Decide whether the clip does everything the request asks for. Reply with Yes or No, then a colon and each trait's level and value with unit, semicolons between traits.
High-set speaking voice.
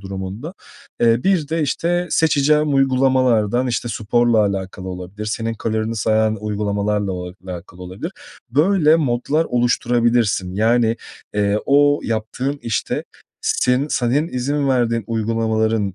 No: low, 115 Hz